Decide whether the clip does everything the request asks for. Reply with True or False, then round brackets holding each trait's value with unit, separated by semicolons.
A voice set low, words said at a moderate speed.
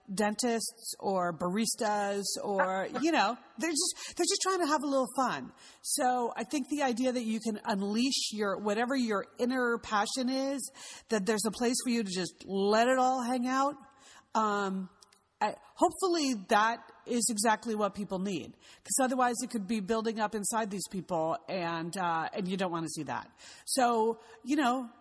False (230 Hz; 180 wpm)